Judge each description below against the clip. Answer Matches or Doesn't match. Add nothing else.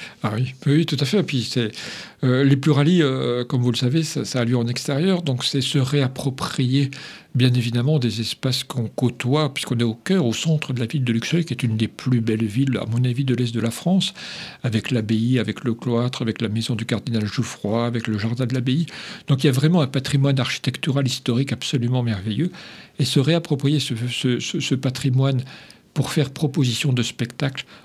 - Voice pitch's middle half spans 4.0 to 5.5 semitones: Doesn't match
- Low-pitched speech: Matches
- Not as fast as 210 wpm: Doesn't match